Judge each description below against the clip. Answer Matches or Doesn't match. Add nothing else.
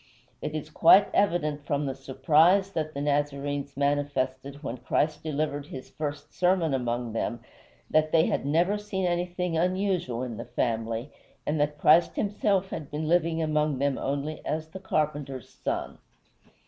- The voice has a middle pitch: Matches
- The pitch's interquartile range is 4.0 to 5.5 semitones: Doesn't match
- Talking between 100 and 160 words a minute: Matches